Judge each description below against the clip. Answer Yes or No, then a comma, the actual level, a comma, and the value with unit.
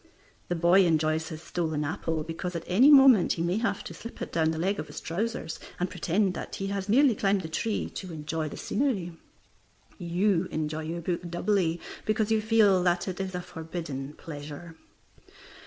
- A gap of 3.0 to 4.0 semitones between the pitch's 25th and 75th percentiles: Yes, average, 3.7 semitones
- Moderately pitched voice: Yes, medium, 175 Hz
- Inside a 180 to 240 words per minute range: Yes, average, 190 wpm